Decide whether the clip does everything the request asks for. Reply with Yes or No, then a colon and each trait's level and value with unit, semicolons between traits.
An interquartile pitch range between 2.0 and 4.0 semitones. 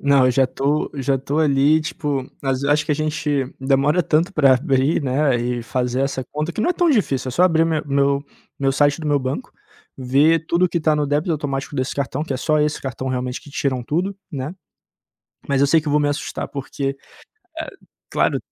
Yes: narrow, 2.4 semitones